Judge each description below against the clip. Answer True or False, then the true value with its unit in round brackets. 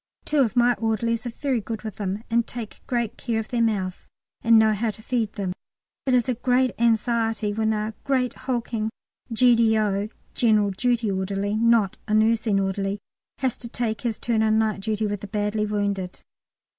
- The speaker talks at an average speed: True (180 wpm)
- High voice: True (220 Hz)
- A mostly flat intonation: True (2.1 semitones)